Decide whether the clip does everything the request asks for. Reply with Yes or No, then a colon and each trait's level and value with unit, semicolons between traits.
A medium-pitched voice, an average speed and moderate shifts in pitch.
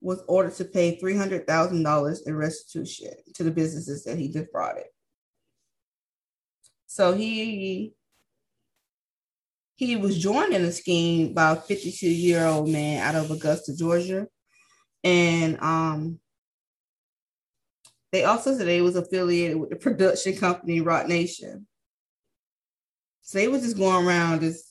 No: medium, 175 Hz; slow, 125 wpm; average, 3.0 semitones